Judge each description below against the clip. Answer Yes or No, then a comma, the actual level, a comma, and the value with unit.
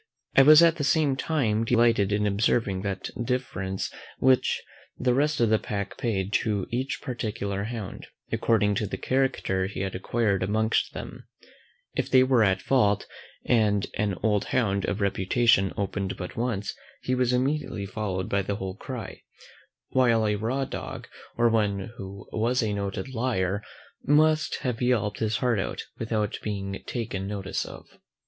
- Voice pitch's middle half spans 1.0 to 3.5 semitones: No, average, 4.0 semitones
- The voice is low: Yes, low, 110 Hz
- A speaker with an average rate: Yes, average, 160 wpm